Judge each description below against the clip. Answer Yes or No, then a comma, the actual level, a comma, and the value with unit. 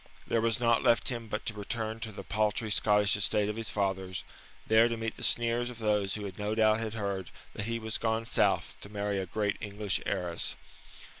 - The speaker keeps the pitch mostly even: Yes, narrow, 2.0 semitones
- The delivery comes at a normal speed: No, fast, 215 wpm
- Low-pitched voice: Yes, low, 110 Hz